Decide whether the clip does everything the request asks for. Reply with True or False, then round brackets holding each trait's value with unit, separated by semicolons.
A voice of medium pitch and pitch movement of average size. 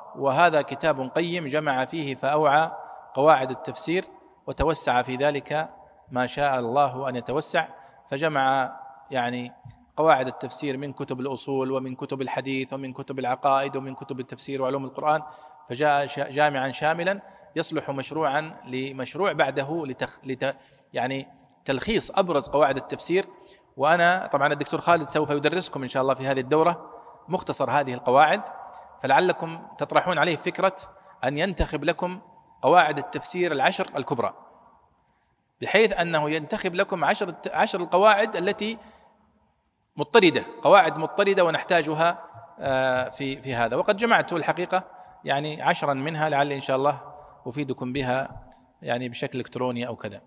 True (145 Hz; 4.1 semitones)